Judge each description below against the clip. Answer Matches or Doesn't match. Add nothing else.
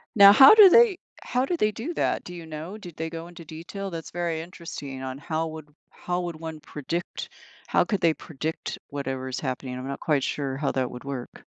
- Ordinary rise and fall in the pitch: Matches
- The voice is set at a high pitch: Doesn't match